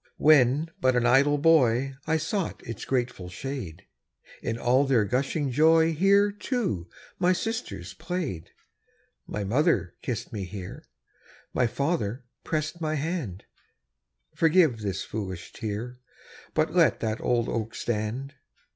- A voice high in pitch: No, low, 130 Hz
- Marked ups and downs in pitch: Yes, wide, 6.4 semitones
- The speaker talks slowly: Yes, slow, 130 wpm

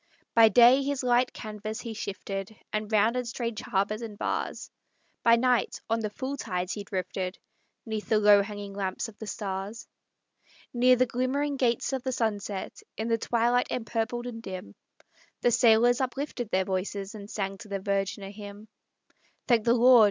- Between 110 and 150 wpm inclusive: No, average, 170 wpm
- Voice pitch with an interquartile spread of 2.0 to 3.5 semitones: Yes, average, 3.1 semitones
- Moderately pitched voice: No, high, 220 Hz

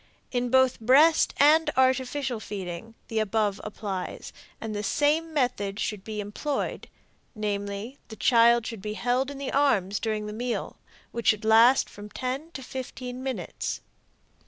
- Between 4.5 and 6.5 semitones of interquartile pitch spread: No, average, 3.7 semitones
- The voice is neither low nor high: No, high, 235 Hz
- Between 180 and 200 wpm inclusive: No, average, 150 wpm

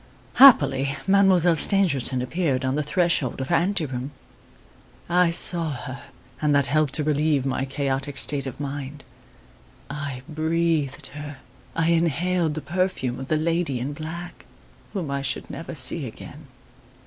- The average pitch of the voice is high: No, medium, 150 Hz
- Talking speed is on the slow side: No, average, 150 wpm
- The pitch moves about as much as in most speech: Yes, average, 3.7 semitones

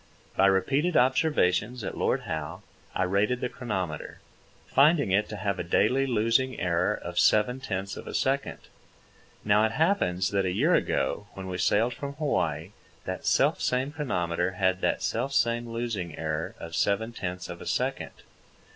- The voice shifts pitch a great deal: Yes, wide, 5.7 semitones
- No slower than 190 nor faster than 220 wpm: No, average, 160 wpm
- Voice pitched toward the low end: Yes, low, 105 Hz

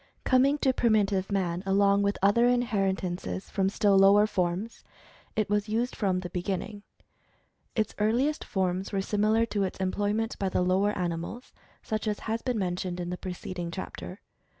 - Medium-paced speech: Yes, average, 160 wpm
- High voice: Yes, high, 200 Hz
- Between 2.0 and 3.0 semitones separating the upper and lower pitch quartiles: Yes, average, 2.7 semitones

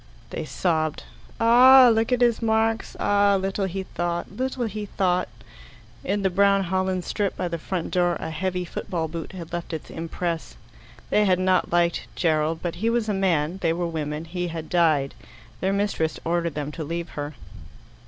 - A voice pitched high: No, medium, 180 Hz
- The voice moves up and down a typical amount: Yes, average, 3.3 semitones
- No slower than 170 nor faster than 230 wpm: Yes, average, 180 wpm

